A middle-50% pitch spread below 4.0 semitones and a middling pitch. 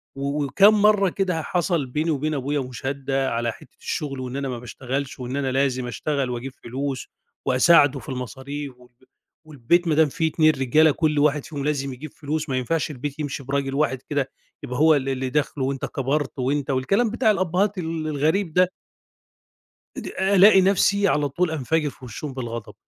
Yes: average, 3.3 semitones; medium, 145 Hz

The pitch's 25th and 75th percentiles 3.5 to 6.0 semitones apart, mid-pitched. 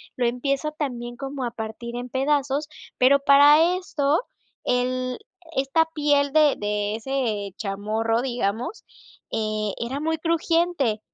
No: average, 4.2 semitones; very high, 260 Hz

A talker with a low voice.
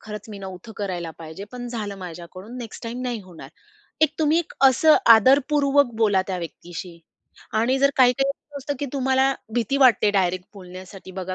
No: high, 220 Hz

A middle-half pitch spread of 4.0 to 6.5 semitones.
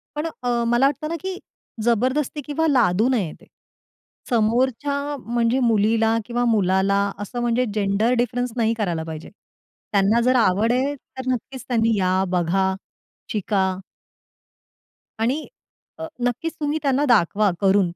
Yes: average, 4.3 semitones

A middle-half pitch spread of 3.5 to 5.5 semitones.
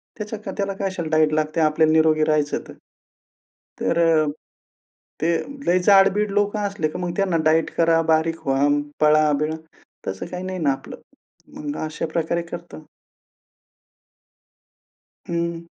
No: narrow, 2.6 semitones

